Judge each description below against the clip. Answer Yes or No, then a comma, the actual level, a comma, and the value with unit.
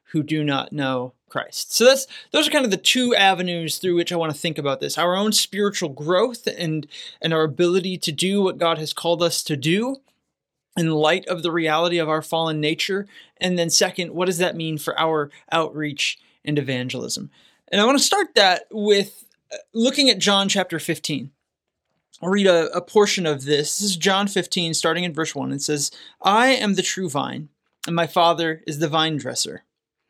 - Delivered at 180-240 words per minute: Yes, average, 200 wpm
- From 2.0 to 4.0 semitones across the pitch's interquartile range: Yes, average, 3.7 semitones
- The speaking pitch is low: No, medium, 170 Hz